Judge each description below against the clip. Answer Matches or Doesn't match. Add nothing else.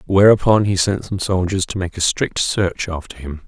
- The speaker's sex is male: Matches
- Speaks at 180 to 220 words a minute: Matches